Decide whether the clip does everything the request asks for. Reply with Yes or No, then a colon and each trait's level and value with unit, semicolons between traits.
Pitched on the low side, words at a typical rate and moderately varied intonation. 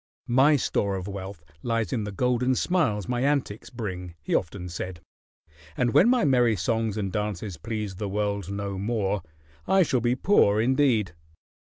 Yes: low, 105 Hz; average, 165 wpm; average, 4.1 semitones